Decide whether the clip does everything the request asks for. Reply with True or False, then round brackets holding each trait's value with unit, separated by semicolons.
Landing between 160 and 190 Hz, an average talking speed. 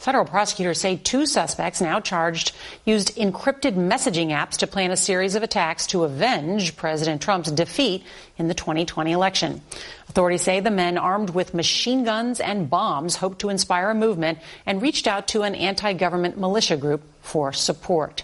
True (185 Hz; 170 wpm)